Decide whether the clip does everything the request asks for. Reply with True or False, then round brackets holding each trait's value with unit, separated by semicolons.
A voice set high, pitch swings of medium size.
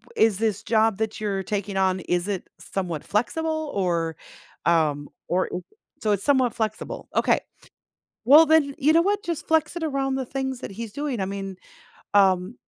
False (220 Hz; 6.5 semitones)